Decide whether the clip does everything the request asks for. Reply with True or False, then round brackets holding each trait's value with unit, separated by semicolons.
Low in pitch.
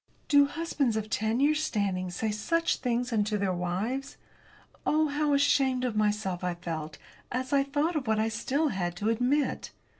False (235 Hz)